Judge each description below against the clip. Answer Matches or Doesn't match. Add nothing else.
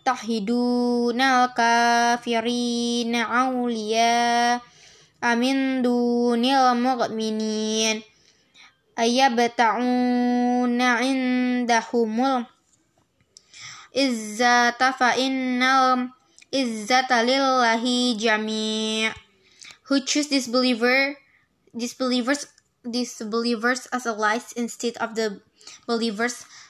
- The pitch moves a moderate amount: Doesn't match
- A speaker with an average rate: Doesn't match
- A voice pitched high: Matches